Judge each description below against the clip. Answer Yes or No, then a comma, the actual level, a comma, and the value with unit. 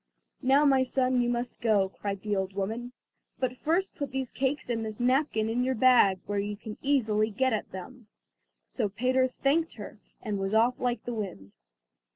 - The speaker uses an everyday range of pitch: Yes, average, 3.8 semitones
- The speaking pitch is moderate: No, high, 240 Hz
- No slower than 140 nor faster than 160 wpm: No, average, 190 wpm